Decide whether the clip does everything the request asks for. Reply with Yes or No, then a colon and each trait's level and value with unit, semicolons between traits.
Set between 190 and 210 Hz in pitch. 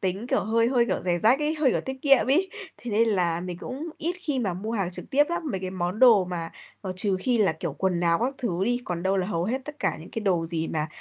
Yes: high, 200 Hz